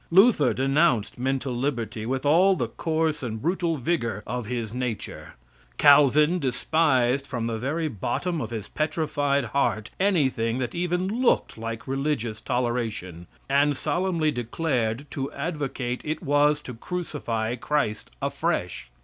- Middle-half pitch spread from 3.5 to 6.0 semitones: Yes, average, 4.8 semitones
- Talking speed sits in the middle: No, slow, 130 wpm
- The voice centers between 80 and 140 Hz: Yes, low, 135 Hz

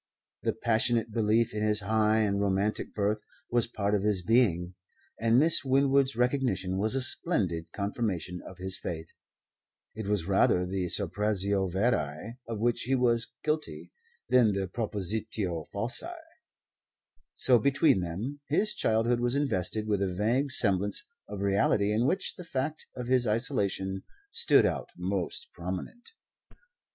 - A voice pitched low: Yes, low, 105 Hz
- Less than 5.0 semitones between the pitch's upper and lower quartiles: Yes, average, 4.2 semitones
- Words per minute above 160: No, average, 140 wpm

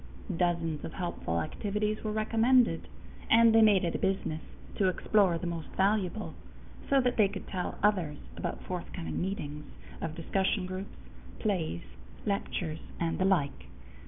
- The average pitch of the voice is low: No, high, 190 Hz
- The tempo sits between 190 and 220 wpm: No, average, 145 wpm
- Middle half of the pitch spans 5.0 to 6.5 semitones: No, average, 4.3 semitones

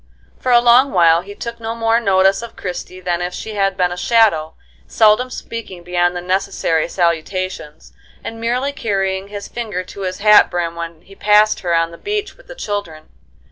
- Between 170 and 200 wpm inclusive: Yes, average, 190 wpm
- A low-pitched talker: No, high, 195 Hz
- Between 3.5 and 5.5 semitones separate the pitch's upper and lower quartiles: Yes, average, 4.4 semitones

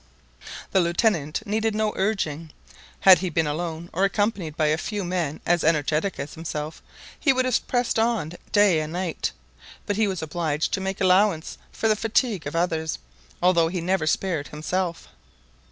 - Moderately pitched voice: Yes, medium, 180 Hz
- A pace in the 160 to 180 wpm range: Yes, average, 170 wpm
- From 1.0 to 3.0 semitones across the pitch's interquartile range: No, average, 4.4 semitones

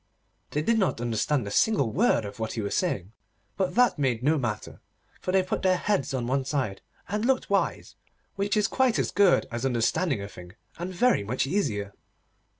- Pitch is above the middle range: No, medium, 140 Hz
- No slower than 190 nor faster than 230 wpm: Yes, average, 195 wpm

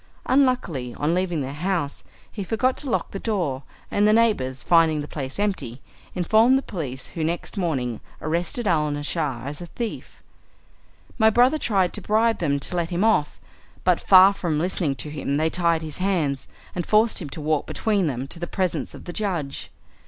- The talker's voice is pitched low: No, medium, 175 Hz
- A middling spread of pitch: No, wide, 5.8 semitones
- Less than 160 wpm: No, average, 185 wpm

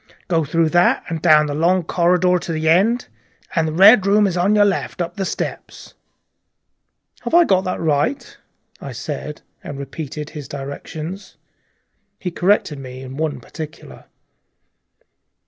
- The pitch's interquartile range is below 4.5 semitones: Yes, average, 3.8 semitones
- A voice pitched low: No, medium, 165 Hz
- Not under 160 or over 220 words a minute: No, average, 150 wpm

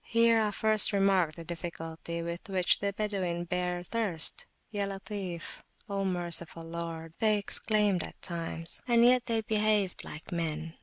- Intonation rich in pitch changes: No, average, 3.8 semitones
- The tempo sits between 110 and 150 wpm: Yes, average, 140 wpm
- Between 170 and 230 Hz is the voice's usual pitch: Yes, medium, 185 Hz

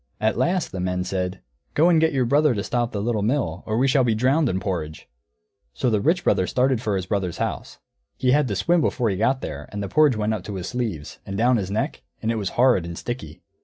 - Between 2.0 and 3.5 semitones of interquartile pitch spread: No, wide, 5.4 semitones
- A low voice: Yes, low, 110 Hz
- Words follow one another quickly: Yes, fast, 245 wpm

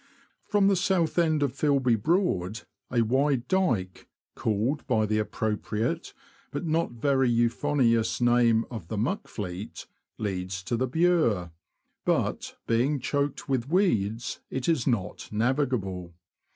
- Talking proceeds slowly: Yes, slow, 130 wpm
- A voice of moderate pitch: No, low, 120 Hz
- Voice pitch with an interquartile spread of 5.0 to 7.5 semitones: Yes, average, 5.3 semitones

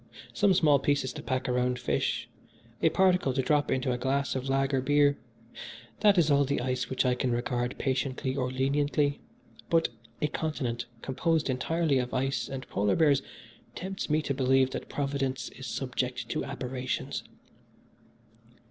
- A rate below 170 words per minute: Yes, average, 155 wpm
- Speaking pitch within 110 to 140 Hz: Yes, low, 135 Hz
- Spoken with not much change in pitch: Yes, narrow, 2.3 semitones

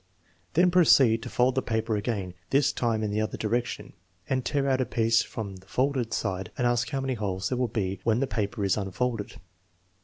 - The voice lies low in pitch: Yes, low, 115 Hz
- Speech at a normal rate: No, fast, 215 wpm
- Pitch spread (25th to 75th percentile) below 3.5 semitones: No, average, 3.8 semitones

